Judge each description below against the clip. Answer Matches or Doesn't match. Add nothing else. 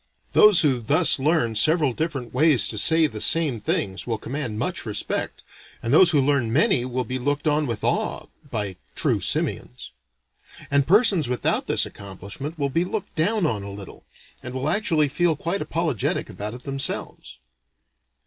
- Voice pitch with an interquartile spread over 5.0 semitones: Matches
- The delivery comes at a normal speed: Matches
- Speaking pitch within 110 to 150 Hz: Matches